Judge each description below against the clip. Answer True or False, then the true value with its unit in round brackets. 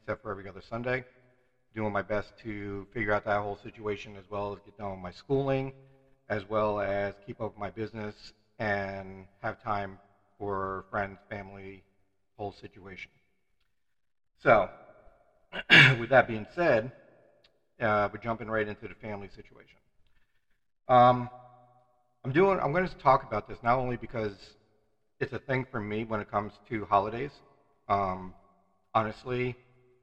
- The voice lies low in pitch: True (105 Hz)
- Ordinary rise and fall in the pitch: True (3.6 semitones)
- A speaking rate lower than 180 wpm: True (150 wpm)